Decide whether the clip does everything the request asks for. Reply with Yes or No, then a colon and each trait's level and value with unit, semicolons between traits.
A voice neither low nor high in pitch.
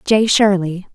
No: high, 195 Hz